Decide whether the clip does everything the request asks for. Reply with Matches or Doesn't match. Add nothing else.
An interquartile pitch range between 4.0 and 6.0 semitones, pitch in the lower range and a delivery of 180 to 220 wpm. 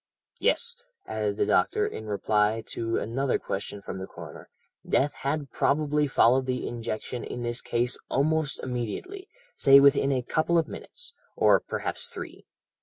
Doesn't match